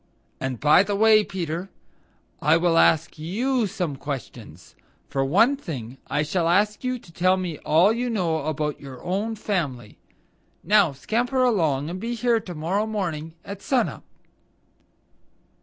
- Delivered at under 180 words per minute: Yes, average, 155 wpm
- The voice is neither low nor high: Yes, medium, 180 Hz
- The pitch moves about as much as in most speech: No, wide, 5.8 semitones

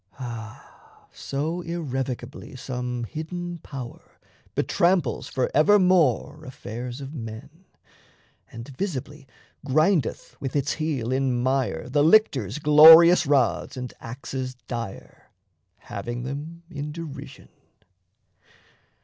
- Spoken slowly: Yes, slow, 95 wpm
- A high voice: No, medium, 140 Hz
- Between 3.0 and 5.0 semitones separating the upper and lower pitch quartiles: Yes, average, 4.2 semitones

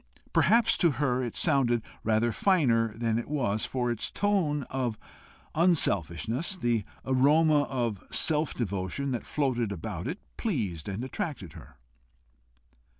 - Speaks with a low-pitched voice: Yes, low, 125 Hz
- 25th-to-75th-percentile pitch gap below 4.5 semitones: No, average, 5.3 semitones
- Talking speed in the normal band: No, slow, 130 wpm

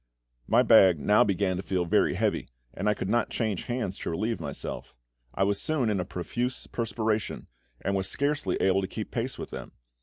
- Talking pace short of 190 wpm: No, average, 200 wpm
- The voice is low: Yes, low, 100 Hz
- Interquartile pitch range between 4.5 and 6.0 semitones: No, average, 3.7 semitones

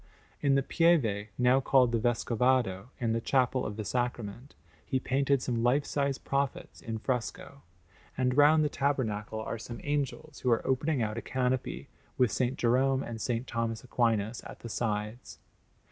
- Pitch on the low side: Yes, low, 125 Hz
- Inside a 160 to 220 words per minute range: Yes, average, 165 wpm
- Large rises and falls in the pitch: No, average, 3.0 semitones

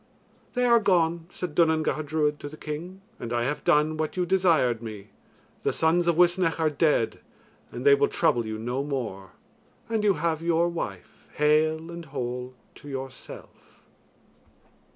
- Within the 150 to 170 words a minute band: Yes, average, 165 wpm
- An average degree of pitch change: Yes, average, 4.4 semitones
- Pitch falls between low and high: Yes, medium, 155 Hz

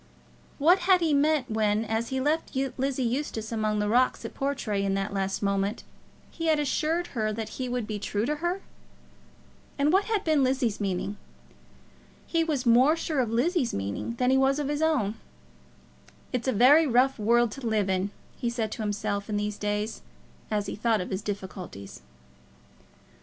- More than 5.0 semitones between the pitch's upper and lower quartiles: Yes, wide, 5.5 semitones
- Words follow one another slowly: No, average, 180 wpm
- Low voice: No, high, 235 Hz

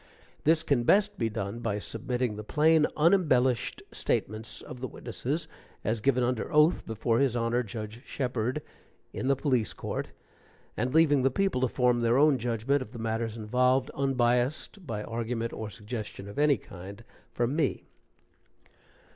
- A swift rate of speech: No, average, 155 wpm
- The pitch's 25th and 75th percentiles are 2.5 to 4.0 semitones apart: Yes, average, 3.4 semitones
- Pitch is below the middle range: Yes, low, 125 Hz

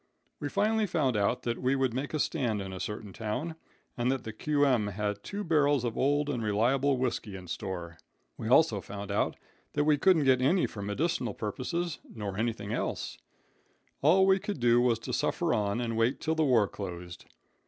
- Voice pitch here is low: Yes, low, 125 Hz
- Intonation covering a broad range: Yes, wide, 5.8 semitones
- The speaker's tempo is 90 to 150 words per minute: No, average, 195 wpm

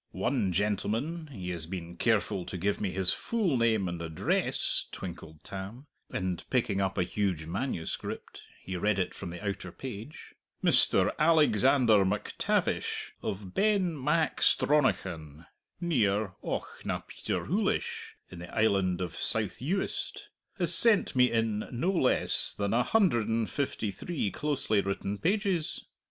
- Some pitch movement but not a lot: No, wide, 6.8 semitones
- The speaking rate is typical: No, slow, 130 wpm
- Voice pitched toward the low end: Yes, low, 105 Hz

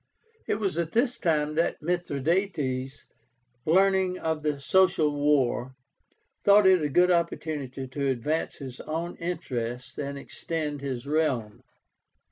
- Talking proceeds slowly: Yes, slow, 125 wpm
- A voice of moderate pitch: Yes, medium, 155 Hz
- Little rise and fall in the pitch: No, average, 4.2 semitones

